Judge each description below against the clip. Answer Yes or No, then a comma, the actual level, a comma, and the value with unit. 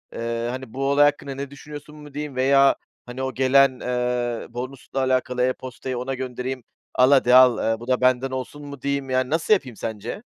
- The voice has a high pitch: No, low, 130 Hz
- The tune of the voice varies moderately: No, narrow, 1.8 semitones